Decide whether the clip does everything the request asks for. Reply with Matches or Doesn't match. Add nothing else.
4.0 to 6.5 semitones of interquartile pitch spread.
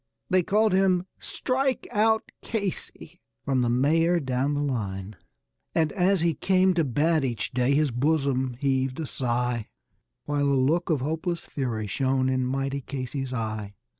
Matches